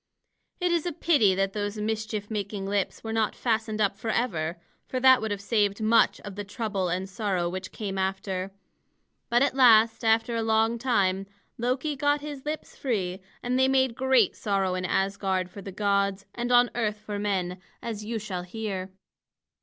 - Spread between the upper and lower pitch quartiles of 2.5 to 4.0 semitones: Yes, average, 3.4 semitones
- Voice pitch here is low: No, high, 210 Hz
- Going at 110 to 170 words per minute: No, average, 180 wpm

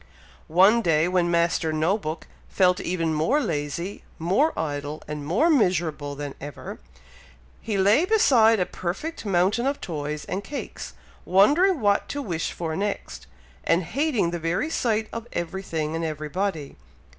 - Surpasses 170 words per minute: No, average, 145 wpm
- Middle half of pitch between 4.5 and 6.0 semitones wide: Yes, wide, 5.5 semitones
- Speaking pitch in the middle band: Yes, medium, 180 Hz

